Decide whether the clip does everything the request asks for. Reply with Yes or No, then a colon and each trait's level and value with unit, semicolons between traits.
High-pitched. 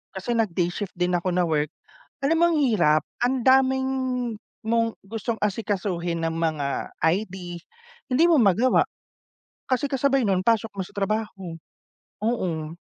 Yes: high, 200 Hz